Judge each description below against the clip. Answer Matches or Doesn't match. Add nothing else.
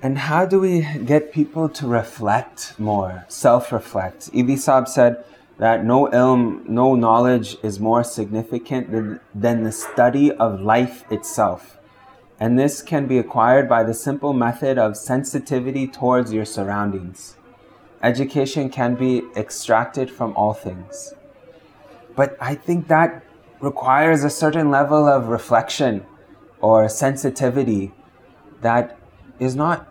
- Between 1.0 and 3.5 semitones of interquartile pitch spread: Doesn't match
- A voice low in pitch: Matches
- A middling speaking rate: Doesn't match